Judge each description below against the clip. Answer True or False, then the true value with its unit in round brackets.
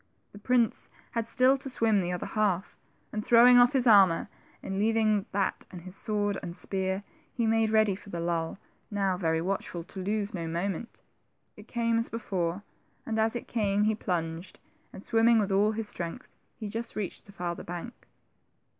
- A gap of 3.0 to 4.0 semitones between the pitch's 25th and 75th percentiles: True (3.5 semitones)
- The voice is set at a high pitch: True (205 Hz)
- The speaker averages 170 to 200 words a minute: True (180 wpm)